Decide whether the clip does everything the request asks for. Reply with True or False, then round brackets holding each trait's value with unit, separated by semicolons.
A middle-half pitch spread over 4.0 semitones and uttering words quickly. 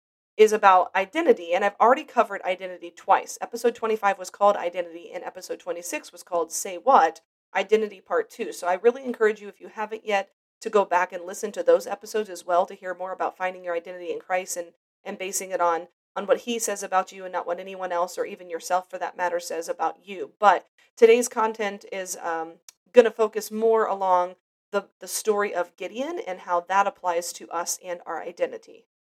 False (3.7 semitones; 210 wpm)